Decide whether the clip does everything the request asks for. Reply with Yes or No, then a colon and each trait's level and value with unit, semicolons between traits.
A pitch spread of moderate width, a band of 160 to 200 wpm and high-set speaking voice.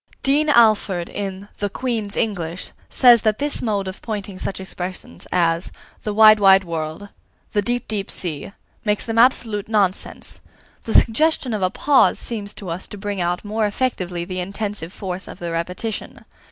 Yes: average, 3.3 semitones; average, 165 wpm; high, 205 Hz